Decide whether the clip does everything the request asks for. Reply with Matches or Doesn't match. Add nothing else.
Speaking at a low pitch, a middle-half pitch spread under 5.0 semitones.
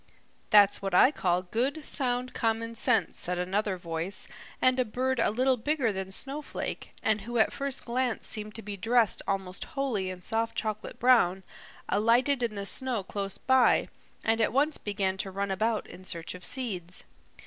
Doesn't match